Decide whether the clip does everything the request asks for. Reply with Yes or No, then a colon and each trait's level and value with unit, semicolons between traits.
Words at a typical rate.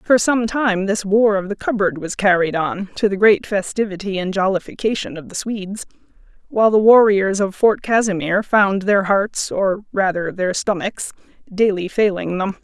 Yes: average, 170 wpm